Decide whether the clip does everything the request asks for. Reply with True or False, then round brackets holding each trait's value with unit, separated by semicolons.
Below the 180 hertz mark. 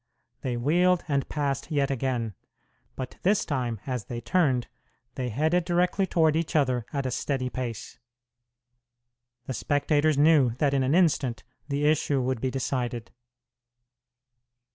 True (140 Hz)